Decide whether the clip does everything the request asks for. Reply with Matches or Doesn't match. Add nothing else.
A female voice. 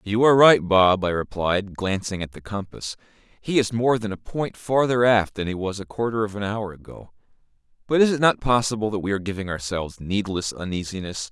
Doesn't match